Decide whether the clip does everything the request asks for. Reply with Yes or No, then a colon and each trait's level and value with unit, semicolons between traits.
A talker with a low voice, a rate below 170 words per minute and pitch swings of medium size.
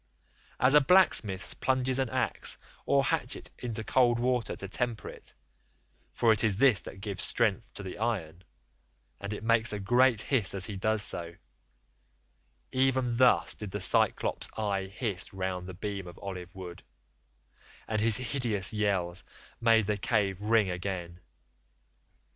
Yes: low, 105 Hz; average, 145 wpm; average, 3.9 semitones